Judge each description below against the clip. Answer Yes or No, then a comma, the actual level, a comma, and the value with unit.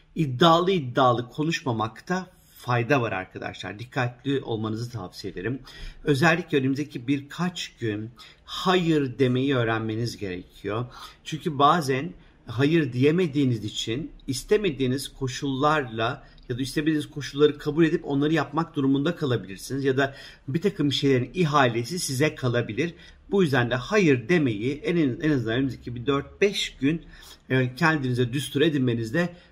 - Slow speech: No, average, 120 wpm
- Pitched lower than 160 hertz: Yes, medium, 140 Hz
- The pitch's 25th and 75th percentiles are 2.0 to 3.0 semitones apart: No, average, 4.1 semitones